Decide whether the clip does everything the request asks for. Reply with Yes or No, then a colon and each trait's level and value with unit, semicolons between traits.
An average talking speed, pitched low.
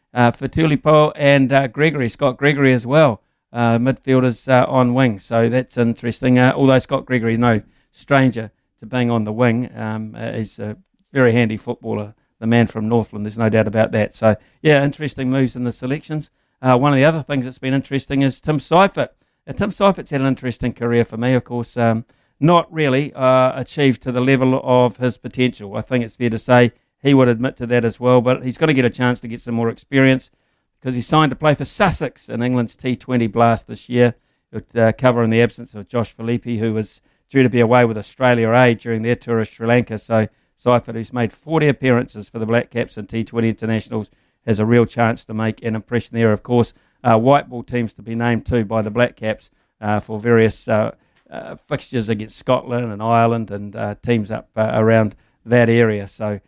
No: fast, 215 wpm; low, 120 Hz